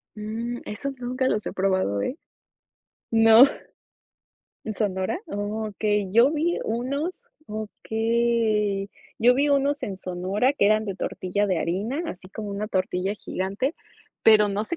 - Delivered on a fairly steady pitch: No, average, 3.5 semitones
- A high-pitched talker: Yes, high, 215 Hz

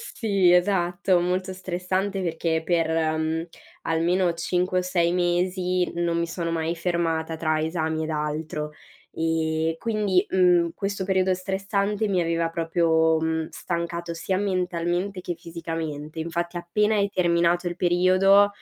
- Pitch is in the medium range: Yes, medium, 175 Hz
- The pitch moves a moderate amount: No, narrow, 2.2 semitones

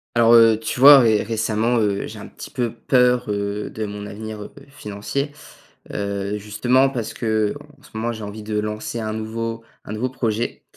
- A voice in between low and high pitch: No, low, 110 Hz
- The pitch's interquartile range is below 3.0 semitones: Yes, narrow, 2.5 semitones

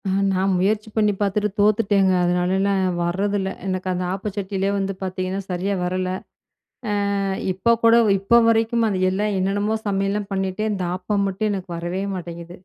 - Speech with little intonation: Yes, narrow, 1.9 semitones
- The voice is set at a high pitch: Yes, high, 195 Hz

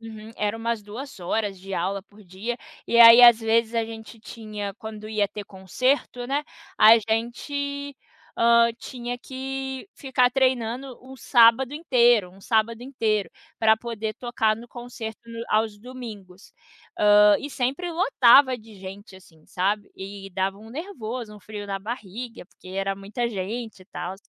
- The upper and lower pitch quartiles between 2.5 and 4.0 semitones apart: Yes, average, 3.1 semitones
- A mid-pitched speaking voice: No, high, 225 Hz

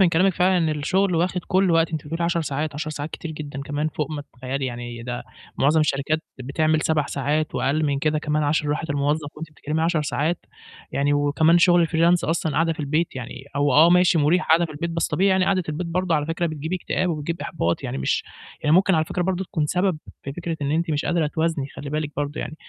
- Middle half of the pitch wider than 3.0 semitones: No, average, 2.7 semitones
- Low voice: No, medium, 155 Hz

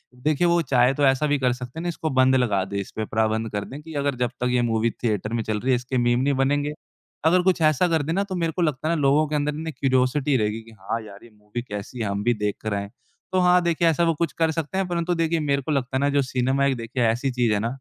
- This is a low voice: Yes, low, 130 Hz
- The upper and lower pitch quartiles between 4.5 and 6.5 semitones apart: Yes, average, 5.1 semitones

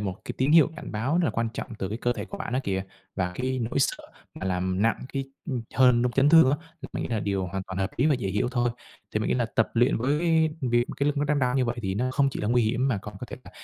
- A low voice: Yes, low, 120 Hz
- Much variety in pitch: No, average, 4.3 semitones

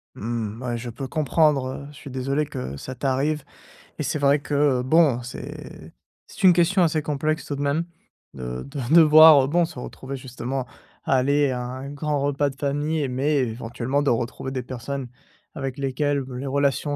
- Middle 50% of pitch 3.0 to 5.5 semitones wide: No, narrow, 2.6 semitones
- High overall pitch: No, medium, 140 Hz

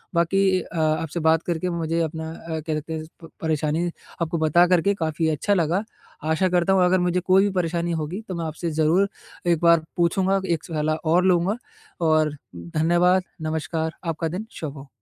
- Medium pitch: Yes, medium, 165 Hz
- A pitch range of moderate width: No, narrow, 2.1 semitones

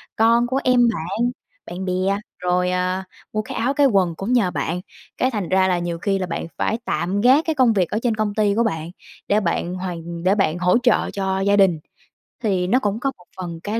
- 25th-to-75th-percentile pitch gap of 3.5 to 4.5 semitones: Yes, average, 3.9 semitones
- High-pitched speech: Yes, high, 195 Hz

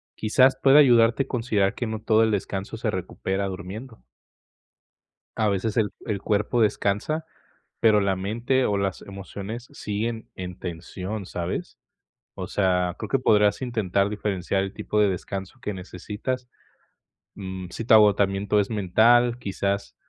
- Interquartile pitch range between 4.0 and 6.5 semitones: No, average, 2.8 semitones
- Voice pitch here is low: Yes, low, 105 Hz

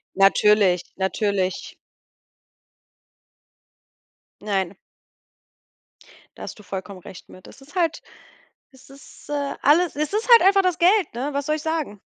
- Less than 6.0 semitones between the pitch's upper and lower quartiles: No, wide, 8.6 semitones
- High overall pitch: Yes, very high, 275 Hz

